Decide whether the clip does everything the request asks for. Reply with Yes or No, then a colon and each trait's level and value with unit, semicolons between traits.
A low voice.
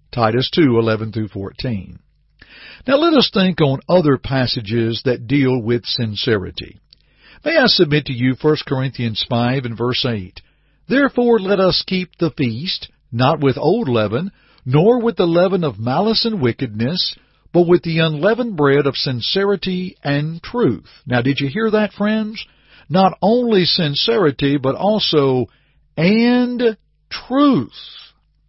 No: medium, 150 Hz